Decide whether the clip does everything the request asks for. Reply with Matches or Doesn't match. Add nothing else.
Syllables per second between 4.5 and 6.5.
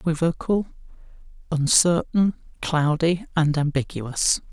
Doesn't match